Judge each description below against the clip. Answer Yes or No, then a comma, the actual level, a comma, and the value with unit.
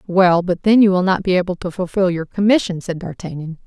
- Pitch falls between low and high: Yes, medium, 180 Hz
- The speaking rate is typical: No, fast, 230 wpm